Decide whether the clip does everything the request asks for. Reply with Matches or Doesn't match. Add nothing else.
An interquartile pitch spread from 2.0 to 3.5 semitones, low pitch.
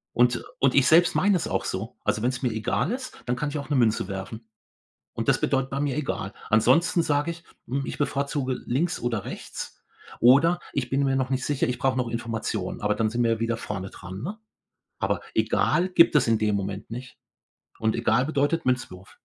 Doesn't match